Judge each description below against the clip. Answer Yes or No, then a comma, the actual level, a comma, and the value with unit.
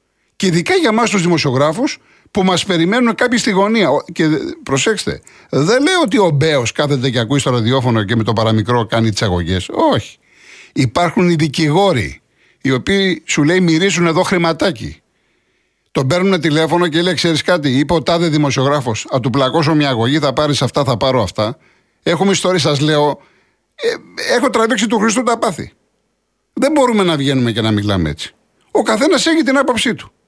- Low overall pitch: No, medium, 160 Hz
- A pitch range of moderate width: No, wide, 6.2 semitones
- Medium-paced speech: No, fast, 175 wpm